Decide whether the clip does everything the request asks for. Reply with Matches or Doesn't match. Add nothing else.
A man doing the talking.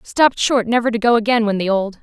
Doesn't match